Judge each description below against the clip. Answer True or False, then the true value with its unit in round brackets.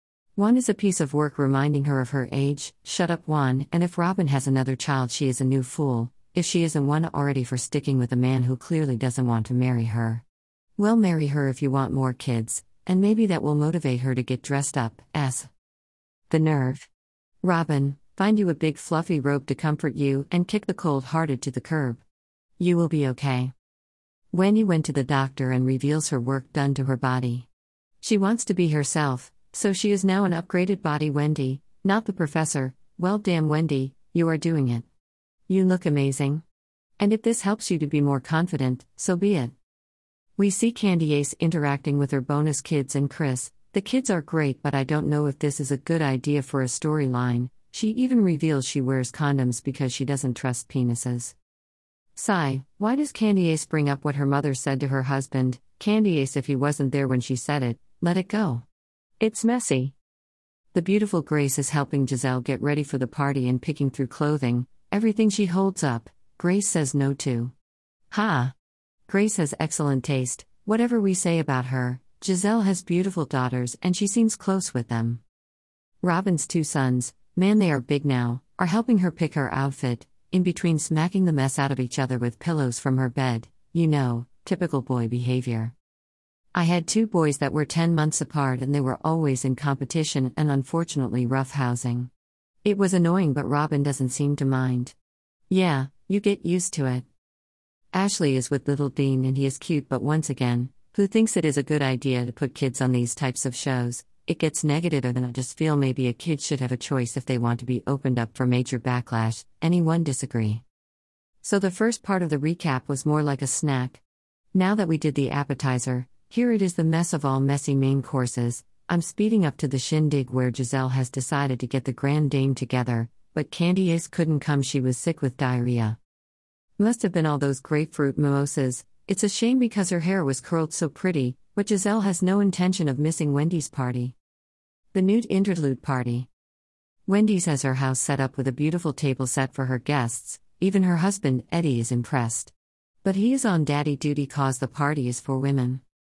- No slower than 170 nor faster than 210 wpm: True (200 wpm)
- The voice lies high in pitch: False (140 Hz)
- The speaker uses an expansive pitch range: False (4.7 semitones)